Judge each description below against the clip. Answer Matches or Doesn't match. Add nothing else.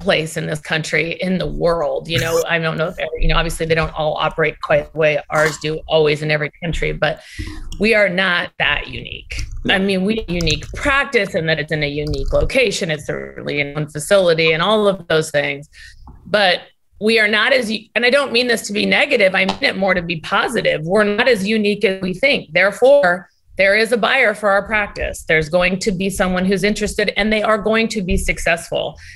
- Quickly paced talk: Matches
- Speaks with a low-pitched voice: Doesn't match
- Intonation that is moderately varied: Matches